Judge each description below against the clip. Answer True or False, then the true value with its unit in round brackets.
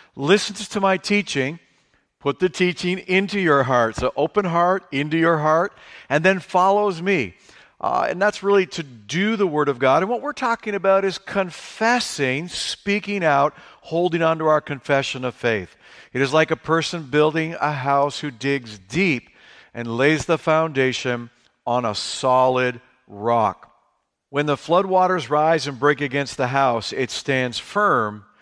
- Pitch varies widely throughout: True (5.7 semitones)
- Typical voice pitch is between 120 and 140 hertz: False (155 Hz)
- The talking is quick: False (165 wpm)